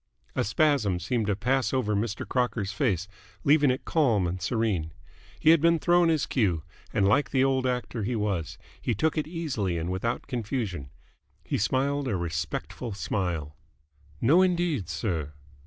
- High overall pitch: No, low, 115 Hz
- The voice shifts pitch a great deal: Yes, wide, 6.8 semitones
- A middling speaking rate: Yes, average, 160 wpm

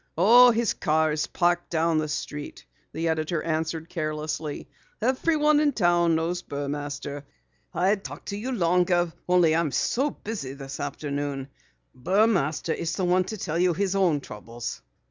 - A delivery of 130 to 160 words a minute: Yes, average, 150 wpm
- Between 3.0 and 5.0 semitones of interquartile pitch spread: Yes, average, 4.0 semitones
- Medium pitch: Yes, medium, 170 Hz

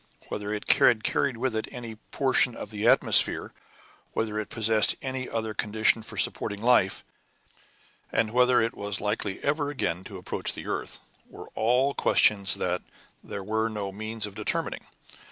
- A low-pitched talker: Yes, low, 110 Hz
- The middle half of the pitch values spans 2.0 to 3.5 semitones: Yes, average, 2.8 semitones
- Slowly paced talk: No, average, 160 wpm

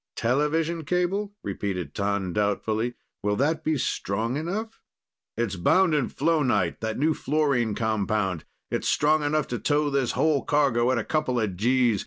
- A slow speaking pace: No, average, 155 wpm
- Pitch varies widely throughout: Yes, wide, 6.5 semitones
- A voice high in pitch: No, low, 130 Hz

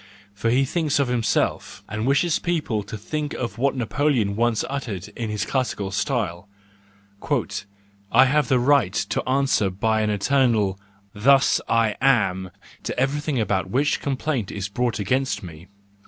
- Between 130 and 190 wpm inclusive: Yes, average, 160 wpm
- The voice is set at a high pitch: No, low, 120 Hz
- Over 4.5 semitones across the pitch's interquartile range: Yes, average, 5.1 semitones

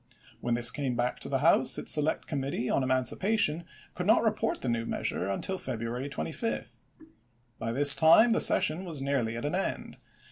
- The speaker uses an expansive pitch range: Yes, wide, 6.4 semitones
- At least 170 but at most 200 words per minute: Yes, average, 180 wpm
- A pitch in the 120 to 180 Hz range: Yes, medium, 140 Hz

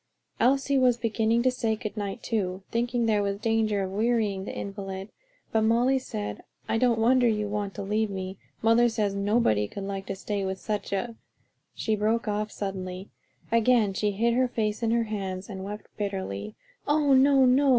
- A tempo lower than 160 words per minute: No, average, 185 wpm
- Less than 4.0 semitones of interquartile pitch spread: Yes, average, 3.1 semitones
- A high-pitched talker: Yes, high, 215 Hz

